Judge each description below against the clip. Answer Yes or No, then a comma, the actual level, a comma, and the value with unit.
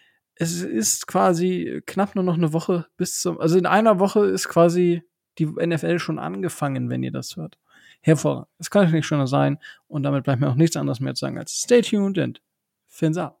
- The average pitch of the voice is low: No, medium, 165 Hz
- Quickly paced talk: Yes, fast, 210 wpm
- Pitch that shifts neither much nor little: Yes, average, 3.5 semitones